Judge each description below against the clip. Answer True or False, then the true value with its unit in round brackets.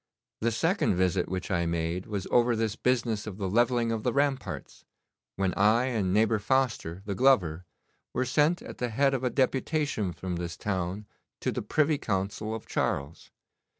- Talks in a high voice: False (110 Hz)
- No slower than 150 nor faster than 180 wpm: True (175 wpm)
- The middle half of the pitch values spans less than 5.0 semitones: False (5.3 semitones)